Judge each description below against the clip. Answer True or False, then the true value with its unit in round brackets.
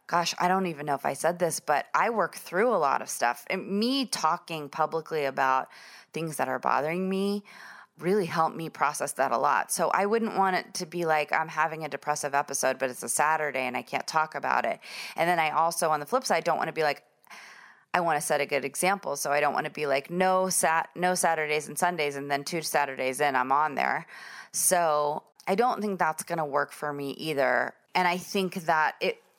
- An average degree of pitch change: True (4.0 semitones)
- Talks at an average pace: False (230 wpm)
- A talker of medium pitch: True (160 Hz)